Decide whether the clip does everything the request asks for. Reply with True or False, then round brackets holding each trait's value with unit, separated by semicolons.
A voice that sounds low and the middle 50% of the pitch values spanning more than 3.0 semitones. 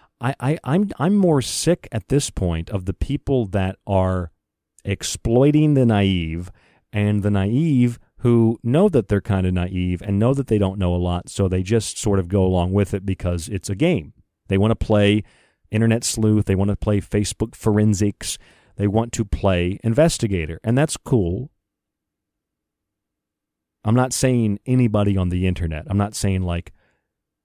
True (105 Hz; 4.0 semitones)